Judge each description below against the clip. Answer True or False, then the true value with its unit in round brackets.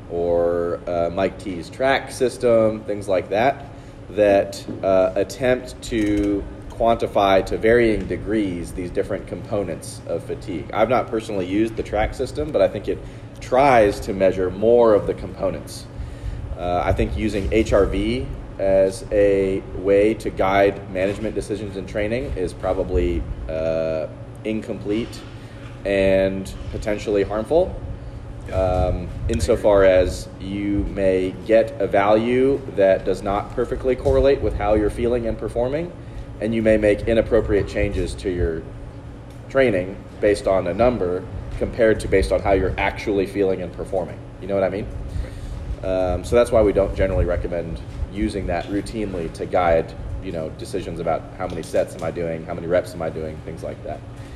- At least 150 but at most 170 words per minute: True (155 wpm)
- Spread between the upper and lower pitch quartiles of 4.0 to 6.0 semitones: False (2.9 semitones)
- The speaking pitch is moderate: False (100 Hz)